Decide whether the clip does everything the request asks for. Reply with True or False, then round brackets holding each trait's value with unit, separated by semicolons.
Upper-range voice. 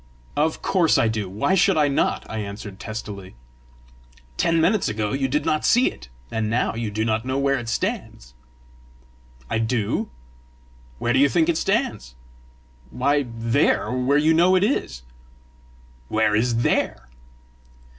False (120 Hz)